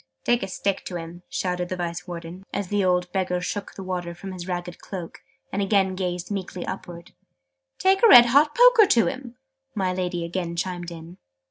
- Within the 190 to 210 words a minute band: Yes, average, 195 wpm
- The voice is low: No, medium, 185 Hz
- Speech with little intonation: Yes, narrow, 2.2 semitones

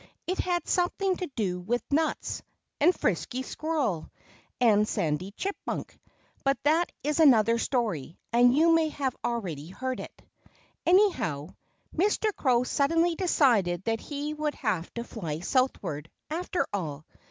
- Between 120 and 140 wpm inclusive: Yes, slow, 135 wpm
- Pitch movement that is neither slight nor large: No, wide, 8.9 semitones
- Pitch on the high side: Yes, very high, 255 Hz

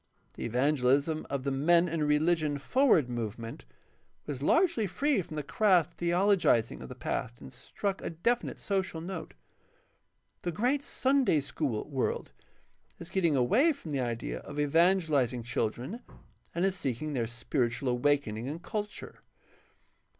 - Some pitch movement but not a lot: No, wide, 6.8 semitones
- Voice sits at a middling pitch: Yes, medium, 150 Hz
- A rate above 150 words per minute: No, average, 145 wpm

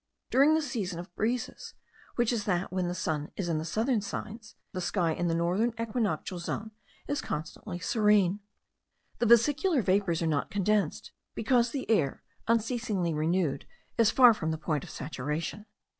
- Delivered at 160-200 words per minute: Yes, average, 165 wpm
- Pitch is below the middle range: No, high, 200 Hz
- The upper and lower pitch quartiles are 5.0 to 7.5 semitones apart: Yes, average, 5.3 semitones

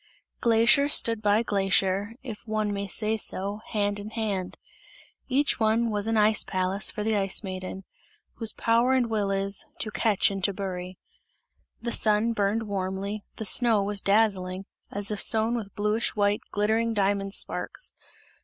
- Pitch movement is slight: Yes, narrow, 2.2 semitones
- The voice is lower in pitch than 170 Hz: No, high, 210 Hz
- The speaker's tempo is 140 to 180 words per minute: Yes, average, 160 wpm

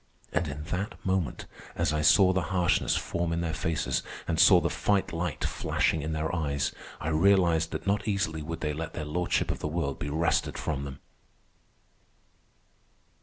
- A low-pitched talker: Yes, very low, 80 Hz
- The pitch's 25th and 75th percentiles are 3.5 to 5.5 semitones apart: No, average, 2.7 semitones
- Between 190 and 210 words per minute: No, average, 175 wpm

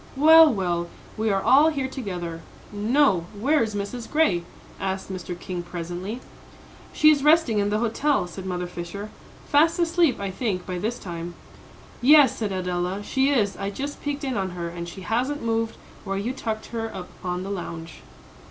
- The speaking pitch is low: No, high, 205 Hz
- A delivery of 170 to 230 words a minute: Yes, average, 180 wpm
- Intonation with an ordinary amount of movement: No, wide, 6.7 semitones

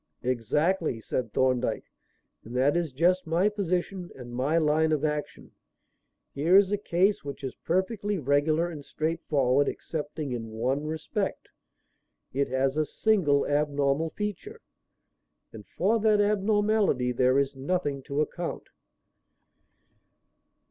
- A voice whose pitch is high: No, medium, 155 Hz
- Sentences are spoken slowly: Yes, slow, 125 wpm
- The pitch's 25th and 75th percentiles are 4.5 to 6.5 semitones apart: Yes, average, 5.2 semitones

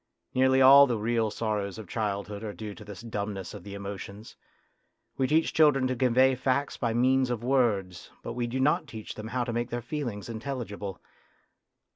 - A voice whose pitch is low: Yes, low, 115 Hz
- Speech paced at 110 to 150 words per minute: No, average, 190 wpm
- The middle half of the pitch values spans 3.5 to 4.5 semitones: Yes, average, 3.9 semitones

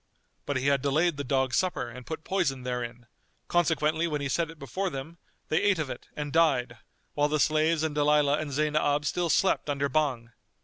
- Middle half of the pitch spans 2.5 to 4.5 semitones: Yes, average, 2.9 semitones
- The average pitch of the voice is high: No, medium, 150 Hz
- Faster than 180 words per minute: Yes, average, 195 wpm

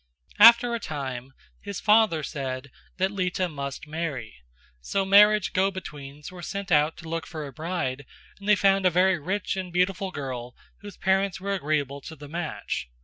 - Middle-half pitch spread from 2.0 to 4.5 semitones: No, average, 5.3 semitones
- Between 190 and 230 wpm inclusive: No, average, 175 wpm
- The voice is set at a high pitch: No, medium, 175 Hz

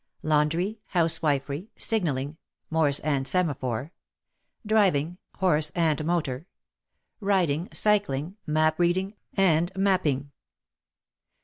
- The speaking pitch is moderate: Yes, medium, 160 Hz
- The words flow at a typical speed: No, slow, 90 wpm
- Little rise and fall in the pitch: No, average, 4.3 semitones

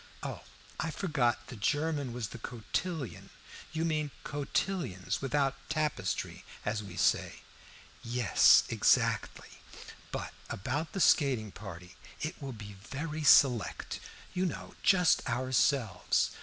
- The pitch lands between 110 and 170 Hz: Yes, low, 135 Hz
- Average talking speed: No, slow, 115 wpm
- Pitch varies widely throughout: Yes, wide, 5.7 semitones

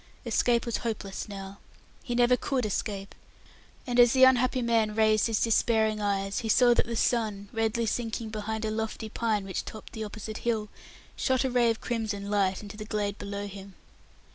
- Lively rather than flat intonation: No, narrow, 2.4 semitones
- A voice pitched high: Yes, high, 220 Hz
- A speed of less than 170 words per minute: No, average, 185 wpm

